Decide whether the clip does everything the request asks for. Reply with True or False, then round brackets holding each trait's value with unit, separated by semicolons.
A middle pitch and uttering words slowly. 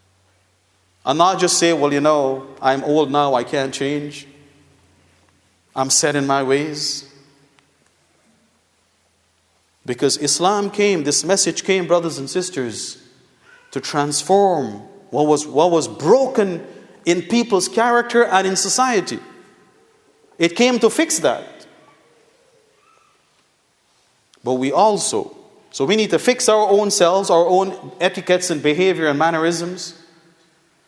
True (165 Hz; 120 wpm)